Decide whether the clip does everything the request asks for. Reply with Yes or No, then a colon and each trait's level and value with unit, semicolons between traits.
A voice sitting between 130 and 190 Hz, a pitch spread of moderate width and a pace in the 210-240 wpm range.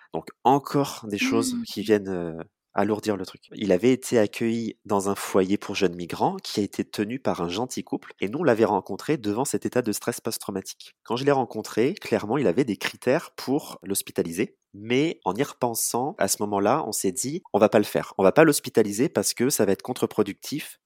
No: low, 105 Hz; average, 3.9 semitones; average, 215 wpm